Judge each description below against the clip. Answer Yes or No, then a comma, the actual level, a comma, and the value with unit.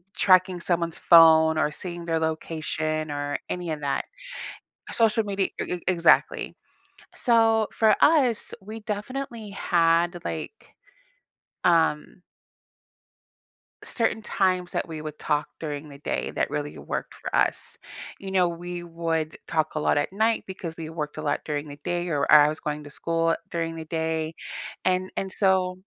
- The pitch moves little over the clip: No, average, 3.2 semitones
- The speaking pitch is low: No, medium, 170 Hz